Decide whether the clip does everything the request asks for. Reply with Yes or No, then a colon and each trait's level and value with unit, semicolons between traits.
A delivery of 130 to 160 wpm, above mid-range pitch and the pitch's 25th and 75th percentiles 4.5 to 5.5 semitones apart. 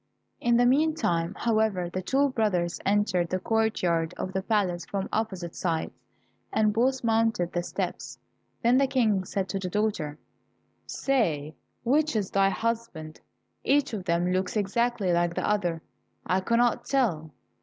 Yes: average, 150 wpm; high, 200 Hz; average, 4.8 semitones